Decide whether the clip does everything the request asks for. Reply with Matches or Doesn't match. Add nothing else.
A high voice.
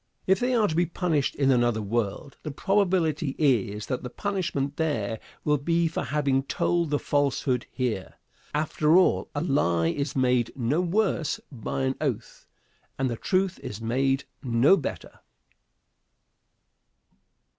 Doesn't match